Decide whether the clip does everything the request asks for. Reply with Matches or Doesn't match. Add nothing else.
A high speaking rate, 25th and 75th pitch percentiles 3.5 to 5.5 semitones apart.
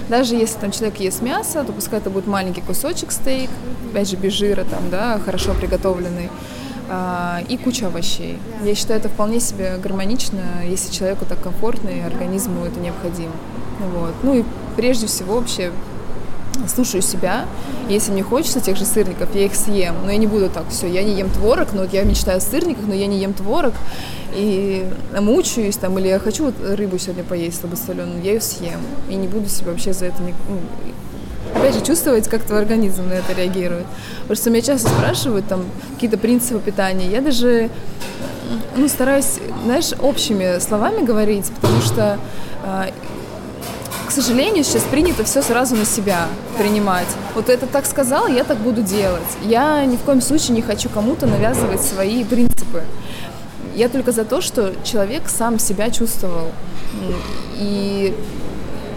Matches